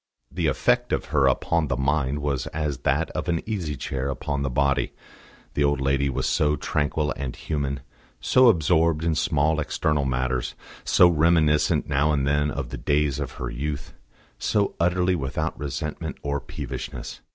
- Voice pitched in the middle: No, very low, 75 Hz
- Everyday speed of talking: Yes, average, 165 wpm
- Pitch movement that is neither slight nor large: No, narrow, 2.3 semitones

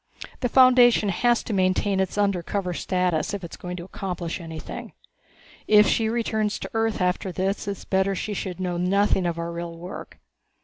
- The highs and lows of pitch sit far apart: No, average, 2.8 semitones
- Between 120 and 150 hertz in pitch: No, high, 190 Hz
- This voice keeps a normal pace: Yes, average, 185 wpm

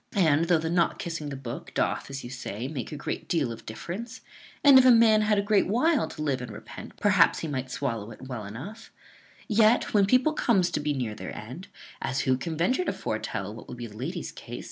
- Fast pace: Yes, fast, 230 wpm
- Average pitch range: No, wide, 8.6 semitones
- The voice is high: No, medium, 155 Hz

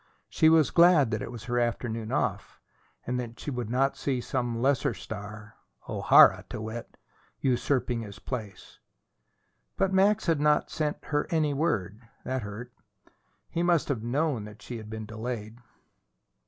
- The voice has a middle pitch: No, low, 125 Hz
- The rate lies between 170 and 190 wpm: No, average, 155 wpm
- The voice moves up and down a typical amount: Yes, average, 5.0 semitones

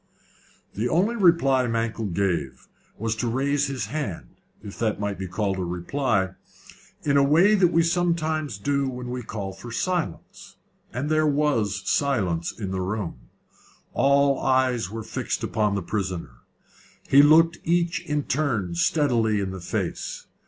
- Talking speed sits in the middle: Yes, average, 150 wpm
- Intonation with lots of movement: Yes, wide, 6.9 semitones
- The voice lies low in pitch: Yes, low, 120 Hz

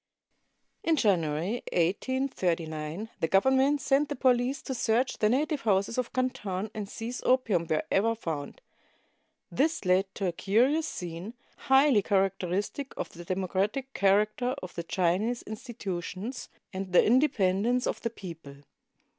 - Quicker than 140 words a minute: No, slow, 135 wpm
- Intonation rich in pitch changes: Yes, wide, 5.7 semitones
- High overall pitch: Yes, high, 210 Hz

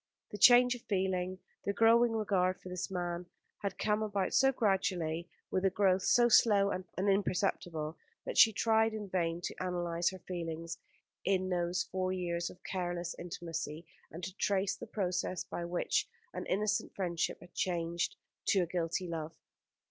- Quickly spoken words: No, average, 165 wpm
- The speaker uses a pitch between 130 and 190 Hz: Yes, medium, 185 Hz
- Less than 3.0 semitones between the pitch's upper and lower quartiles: Yes, narrow, 2.5 semitones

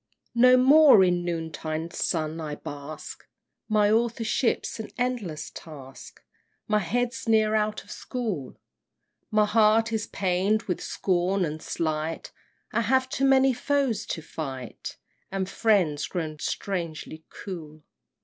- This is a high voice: Yes, high, 195 Hz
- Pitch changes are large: Yes, wide, 6.2 semitones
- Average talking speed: No, slow, 130 wpm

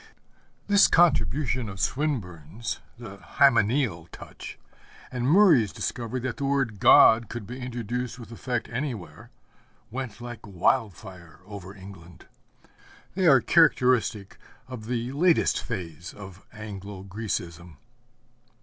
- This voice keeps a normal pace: No, slow, 115 wpm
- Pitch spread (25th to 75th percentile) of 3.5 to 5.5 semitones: Yes, average, 4.9 semitones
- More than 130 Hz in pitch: No, low, 115 Hz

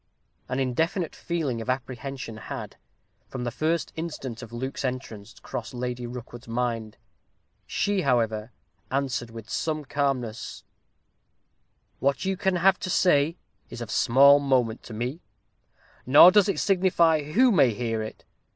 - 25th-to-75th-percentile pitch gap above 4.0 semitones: Yes, average, 5.2 semitones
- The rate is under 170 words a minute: Yes, average, 140 wpm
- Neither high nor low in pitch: No, low, 130 Hz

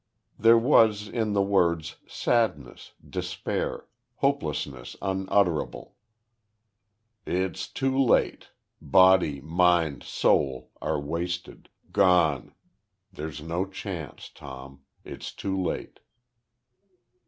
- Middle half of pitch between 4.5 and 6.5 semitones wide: Yes, average, 4.9 semitones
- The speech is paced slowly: Yes, slow, 85 wpm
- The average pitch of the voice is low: Yes, very low, 90 Hz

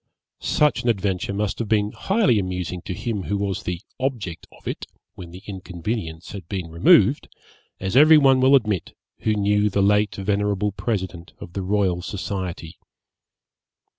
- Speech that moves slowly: No, average, 160 wpm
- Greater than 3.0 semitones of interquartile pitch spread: No, average, 2.7 semitones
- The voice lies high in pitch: No, low, 100 Hz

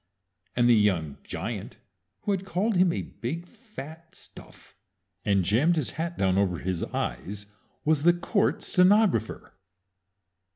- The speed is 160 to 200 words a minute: No, slow, 135 wpm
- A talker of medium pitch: Yes, medium, 155 Hz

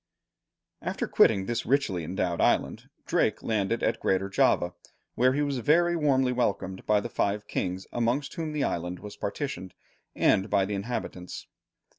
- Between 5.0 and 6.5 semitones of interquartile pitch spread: Yes, wide, 5.6 semitones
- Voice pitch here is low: Yes, low, 105 Hz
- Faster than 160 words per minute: No, average, 155 wpm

